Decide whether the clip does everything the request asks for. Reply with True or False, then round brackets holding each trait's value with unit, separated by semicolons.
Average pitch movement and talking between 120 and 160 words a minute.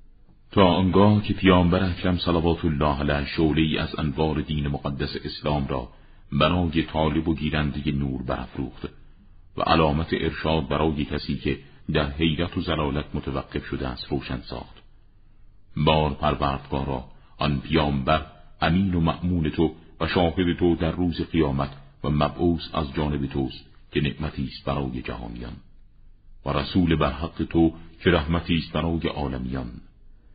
True (3.0 semitones; 140 wpm)